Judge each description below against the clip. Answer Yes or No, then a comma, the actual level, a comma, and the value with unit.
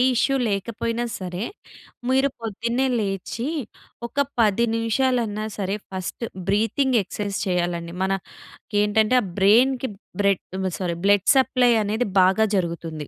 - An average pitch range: Yes, average, 3.9 semitones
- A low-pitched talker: No, high, 210 Hz